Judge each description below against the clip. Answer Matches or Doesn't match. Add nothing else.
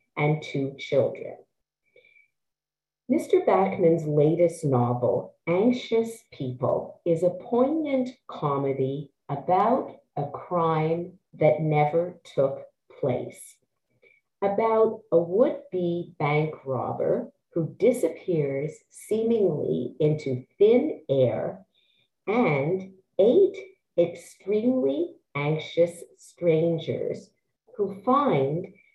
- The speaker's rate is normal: Doesn't match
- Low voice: Doesn't match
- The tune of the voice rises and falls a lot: Matches